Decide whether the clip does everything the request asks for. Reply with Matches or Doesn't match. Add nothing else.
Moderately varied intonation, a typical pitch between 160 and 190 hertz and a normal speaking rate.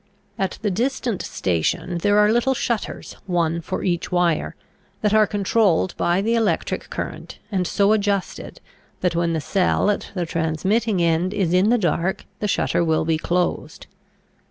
Matches